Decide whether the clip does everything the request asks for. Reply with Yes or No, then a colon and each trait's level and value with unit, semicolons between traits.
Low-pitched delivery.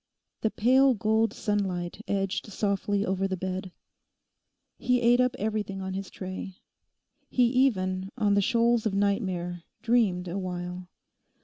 No: high, 200 Hz